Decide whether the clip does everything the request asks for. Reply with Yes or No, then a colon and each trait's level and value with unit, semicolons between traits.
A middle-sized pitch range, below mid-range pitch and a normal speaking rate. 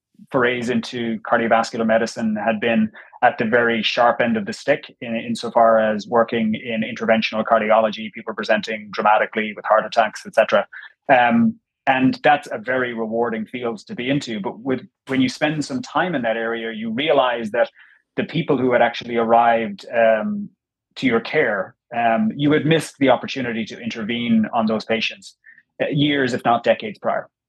Yes: average, 3.9 semitones; low, 120 Hz; average, 170 wpm